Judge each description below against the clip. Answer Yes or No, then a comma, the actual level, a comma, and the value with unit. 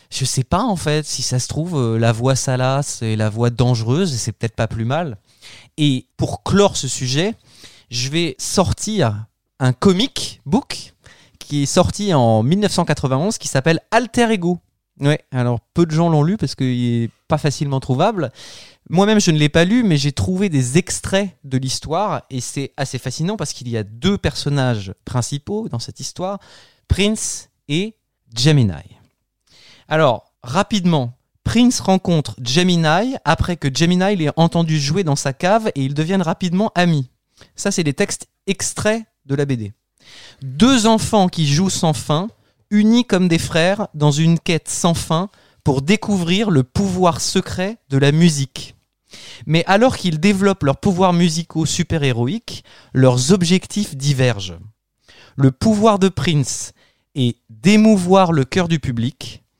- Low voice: No, medium, 150 Hz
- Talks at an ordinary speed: Yes, average, 155 wpm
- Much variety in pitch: Yes, wide, 6.5 semitones